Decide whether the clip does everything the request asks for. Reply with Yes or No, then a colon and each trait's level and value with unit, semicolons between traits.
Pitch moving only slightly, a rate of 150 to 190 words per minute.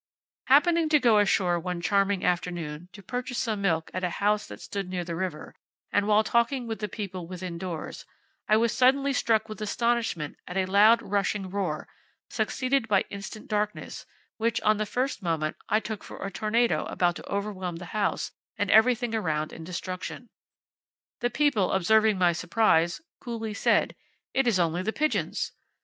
No: average, 4.1 semitones; average, 175 wpm